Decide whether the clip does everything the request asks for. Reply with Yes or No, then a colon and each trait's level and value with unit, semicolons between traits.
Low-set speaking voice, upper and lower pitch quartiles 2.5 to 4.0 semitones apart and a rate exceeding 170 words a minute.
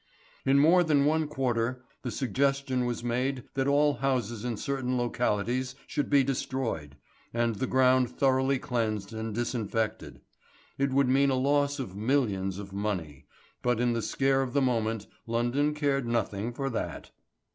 No: low, 125 Hz; average, 3.2 semitones; average, 155 wpm